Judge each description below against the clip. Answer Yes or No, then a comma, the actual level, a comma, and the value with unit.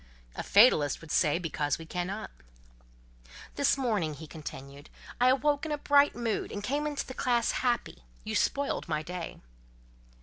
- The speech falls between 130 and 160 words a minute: Yes, average, 145 wpm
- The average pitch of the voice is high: Yes, high, 210 Hz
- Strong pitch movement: Yes, wide, 9.0 semitones